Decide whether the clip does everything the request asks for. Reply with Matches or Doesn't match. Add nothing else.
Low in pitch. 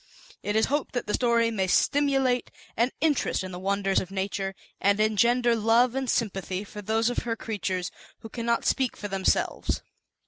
Doesn't match